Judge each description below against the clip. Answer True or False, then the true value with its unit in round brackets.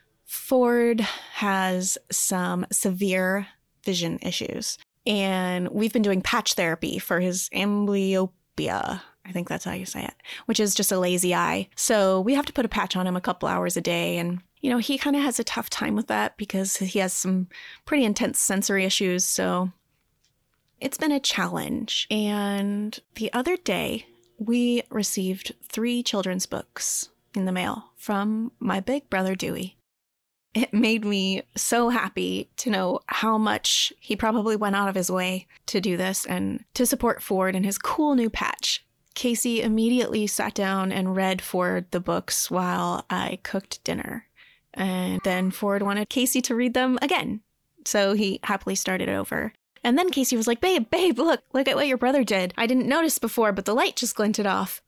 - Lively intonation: False (4.2 semitones)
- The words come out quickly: False (180 wpm)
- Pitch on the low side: False (205 Hz)